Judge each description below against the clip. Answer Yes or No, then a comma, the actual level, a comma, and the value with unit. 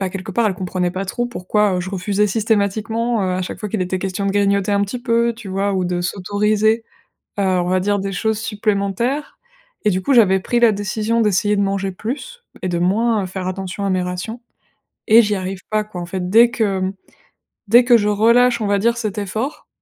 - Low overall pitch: No, high, 205 Hz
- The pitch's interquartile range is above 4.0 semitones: No, average, 2.9 semitones